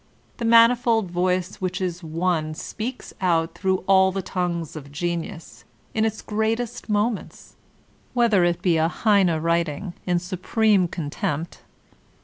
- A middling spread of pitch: Yes, average, 4.0 semitones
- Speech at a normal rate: No, slow, 130 wpm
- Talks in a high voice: No, medium, 180 Hz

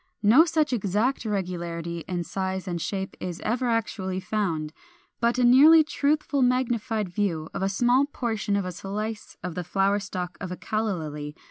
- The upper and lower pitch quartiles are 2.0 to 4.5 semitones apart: No, average, 4.9 semitones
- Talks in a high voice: Yes, high, 200 Hz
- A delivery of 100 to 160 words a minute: No, average, 175 wpm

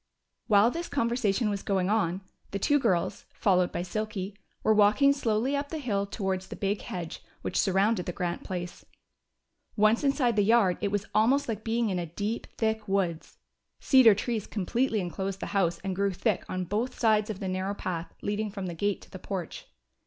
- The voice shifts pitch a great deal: No, average, 3.2 semitones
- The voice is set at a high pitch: Yes, high, 205 Hz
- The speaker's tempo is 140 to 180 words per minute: No, average, 190 wpm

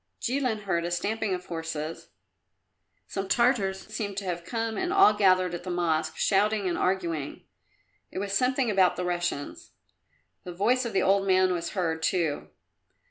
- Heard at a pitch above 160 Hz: Yes, high, 190 Hz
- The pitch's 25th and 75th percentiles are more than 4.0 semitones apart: No, average, 3.4 semitones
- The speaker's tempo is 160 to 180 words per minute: Yes, average, 165 wpm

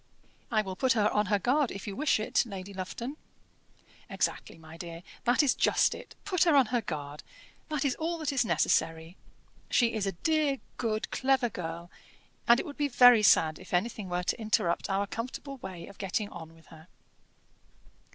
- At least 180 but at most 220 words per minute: Yes, average, 190 wpm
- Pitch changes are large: Yes, wide, 6.4 semitones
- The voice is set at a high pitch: Yes, high, 215 Hz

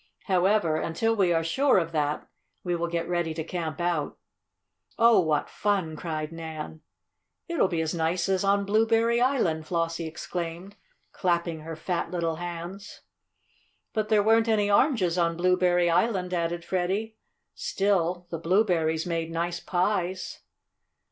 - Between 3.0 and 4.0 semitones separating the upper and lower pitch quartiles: Yes, average, 3.3 semitones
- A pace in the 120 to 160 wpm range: Yes, average, 140 wpm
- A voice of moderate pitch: Yes, medium, 175 Hz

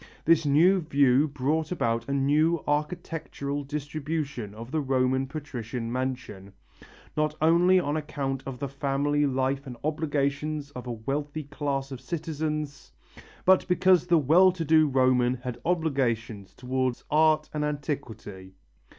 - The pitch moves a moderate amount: Yes, average, 3.1 semitones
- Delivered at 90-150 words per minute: Yes, slow, 135 wpm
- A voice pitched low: No, medium, 145 Hz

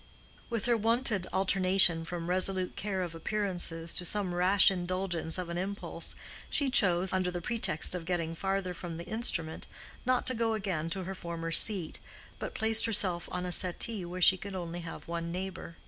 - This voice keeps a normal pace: Yes, average, 180 wpm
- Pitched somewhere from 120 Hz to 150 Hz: No, medium, 185 Hz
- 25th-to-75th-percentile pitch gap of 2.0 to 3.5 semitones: Yes, narrow, 2.6 semitones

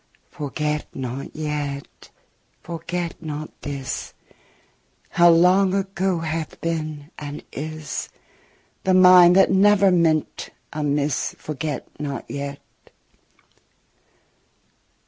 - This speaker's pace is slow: Yes, slow, 90 wpm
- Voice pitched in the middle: Yes, medium, 155 Hz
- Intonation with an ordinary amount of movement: Yes, average, 3.4 semitones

